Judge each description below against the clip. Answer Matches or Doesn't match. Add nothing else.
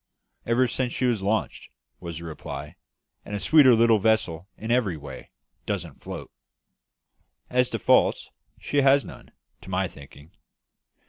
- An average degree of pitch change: Doesn't match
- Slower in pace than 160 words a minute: Matches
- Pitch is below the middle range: Matches